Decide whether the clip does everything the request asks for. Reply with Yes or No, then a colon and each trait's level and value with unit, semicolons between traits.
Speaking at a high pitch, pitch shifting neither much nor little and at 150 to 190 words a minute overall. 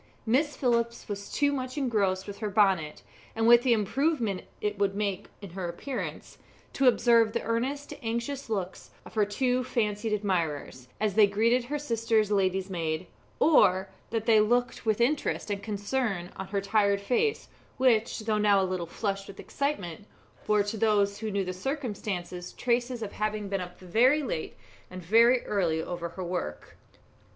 Yes: high, 210 Hz; average, 3.6 semitones; average, 165 wpm